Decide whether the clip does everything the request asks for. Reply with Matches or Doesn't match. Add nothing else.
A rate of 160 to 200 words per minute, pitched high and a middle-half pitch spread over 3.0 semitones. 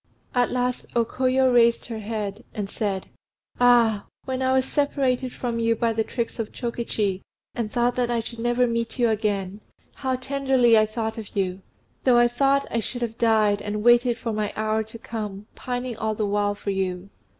Doesn't match